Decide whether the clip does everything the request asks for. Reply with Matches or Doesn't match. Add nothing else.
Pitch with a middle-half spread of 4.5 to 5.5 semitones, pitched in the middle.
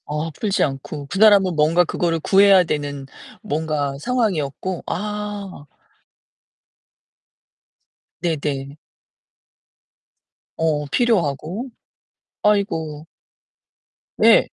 Matches